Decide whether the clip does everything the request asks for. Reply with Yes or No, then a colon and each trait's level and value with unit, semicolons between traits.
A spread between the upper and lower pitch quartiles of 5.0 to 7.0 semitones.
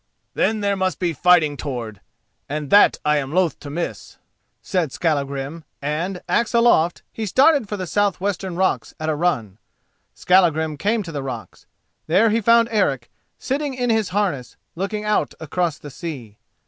Yes: wide, 5.6 semitones